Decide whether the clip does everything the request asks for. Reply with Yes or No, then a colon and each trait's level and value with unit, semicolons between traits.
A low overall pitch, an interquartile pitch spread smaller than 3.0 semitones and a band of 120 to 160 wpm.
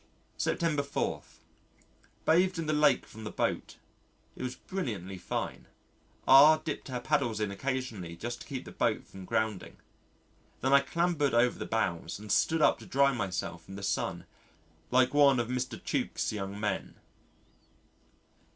No: low, 125 Hz; wide, 5.5 semitones; average, 155 wpm